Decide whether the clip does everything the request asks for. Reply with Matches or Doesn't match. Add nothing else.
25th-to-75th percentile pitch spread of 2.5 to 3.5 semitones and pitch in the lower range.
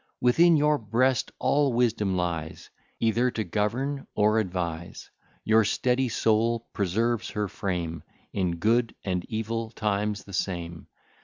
Doesn't match